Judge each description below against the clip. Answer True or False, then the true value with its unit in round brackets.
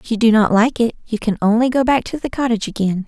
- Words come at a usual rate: False (295 wpm)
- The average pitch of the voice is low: False (230 Hz)